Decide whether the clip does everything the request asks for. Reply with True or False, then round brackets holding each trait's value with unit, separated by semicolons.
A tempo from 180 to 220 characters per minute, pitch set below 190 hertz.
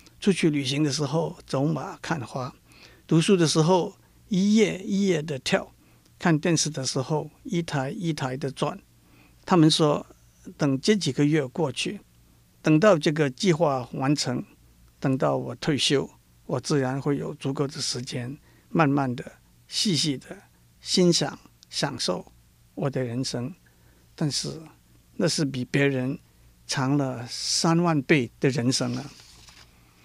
True (195 characters per minute; 135 Hz)